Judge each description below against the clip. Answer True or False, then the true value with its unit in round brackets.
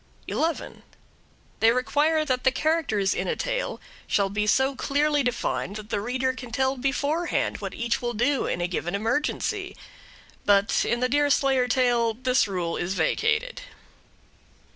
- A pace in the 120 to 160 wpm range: True (150 wpm)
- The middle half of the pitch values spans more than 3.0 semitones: True (4.9 semitones)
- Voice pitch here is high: True (255 Hz)